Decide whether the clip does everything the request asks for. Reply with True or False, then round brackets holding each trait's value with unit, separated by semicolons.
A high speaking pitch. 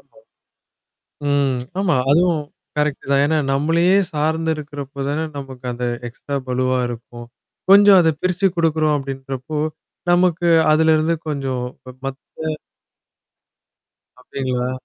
False (150 Hz)